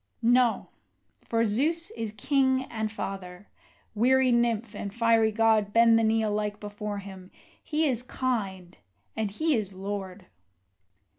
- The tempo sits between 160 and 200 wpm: No, slow, 135 wpm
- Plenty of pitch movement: No, average, 2.7 semitones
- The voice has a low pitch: No, high, 220 Hz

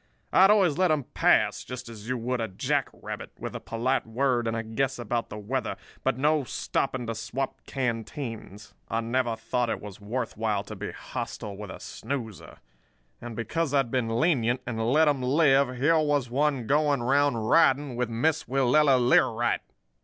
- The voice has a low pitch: Yes, low, 125 Hz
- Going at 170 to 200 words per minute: Yes, average, 185 wpm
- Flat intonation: No, average, 3.6 semitones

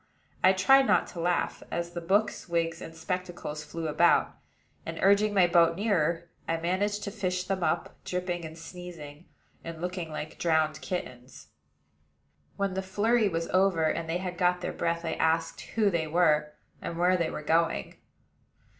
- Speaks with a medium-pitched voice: Yes, medium, 170 Hz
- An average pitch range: No, narrow, 2.3 semitones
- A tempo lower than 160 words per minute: No, average, 170 wpm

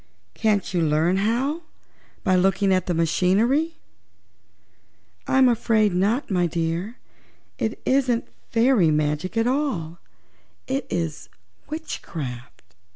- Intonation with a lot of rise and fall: Yes, wide, 6.6 semitones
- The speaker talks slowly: Yes, slow, 105 wpm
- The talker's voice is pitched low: No, high, 195 Hz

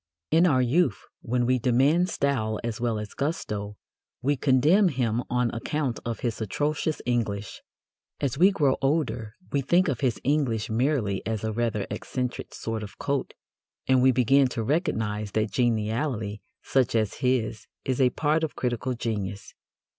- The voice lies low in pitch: Yes, low, 125 Hz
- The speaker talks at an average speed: Yes, average, 160 wpm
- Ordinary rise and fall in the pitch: Yes, average, 4.1 semitones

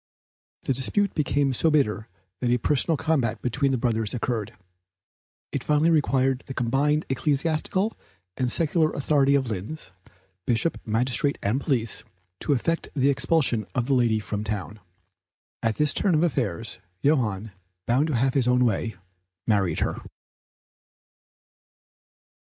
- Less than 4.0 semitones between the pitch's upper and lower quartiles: No, average, 4.6 semitones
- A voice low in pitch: Yes, low, 130 Hz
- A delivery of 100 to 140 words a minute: Yes, slow, 135 wpm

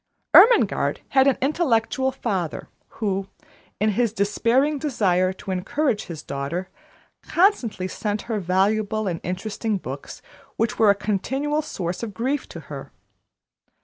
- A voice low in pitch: No, high, 215 Hz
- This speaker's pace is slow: Yes, slow, 130 wpm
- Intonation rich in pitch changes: Yes, wide, 5.8 semitones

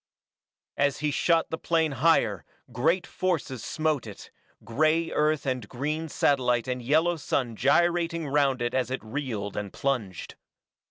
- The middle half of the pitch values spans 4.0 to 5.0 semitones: Yes, average, 4.6 semitones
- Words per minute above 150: No, average, 145 wpm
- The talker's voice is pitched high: No, medium, 140 Hz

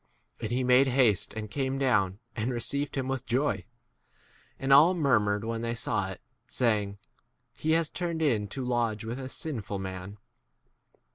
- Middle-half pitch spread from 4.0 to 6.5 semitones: Yes, average, 4.5 semitones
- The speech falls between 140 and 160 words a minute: No, average, 170 wpm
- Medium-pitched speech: No, low, 120 Hz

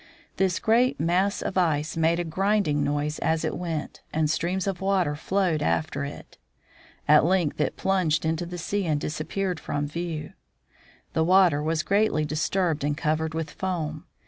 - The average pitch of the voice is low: No, medium, 165 Hz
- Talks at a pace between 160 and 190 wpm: Yes, average, 165 wpm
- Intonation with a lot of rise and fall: No, average, 3.5 semitones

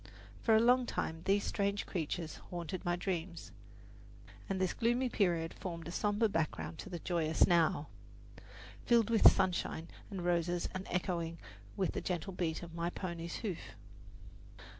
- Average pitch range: Yes, average, 3.0 semitones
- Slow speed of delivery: No, average, 150 wpm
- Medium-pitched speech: Yes, medium, 175 Hz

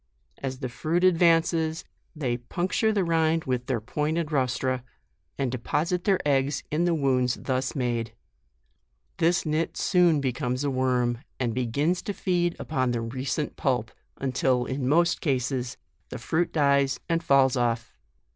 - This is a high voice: No, medium, 140 Hz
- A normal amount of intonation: Yes, average, 4.6 semitones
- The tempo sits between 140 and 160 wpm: Yes, average, 145 wpm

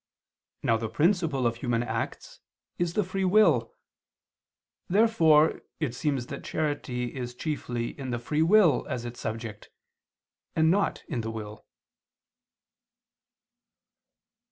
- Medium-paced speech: No, slow, 120 wpm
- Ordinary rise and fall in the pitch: No, wide, 5.7 semitones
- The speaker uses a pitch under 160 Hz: Yes, medium, 140 Hz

